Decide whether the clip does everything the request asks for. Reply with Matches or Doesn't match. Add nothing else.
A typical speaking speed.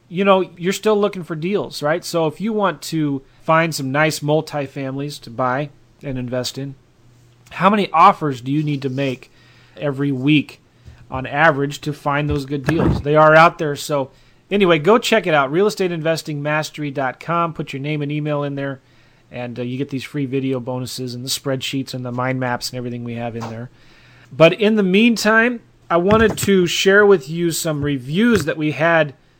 Matches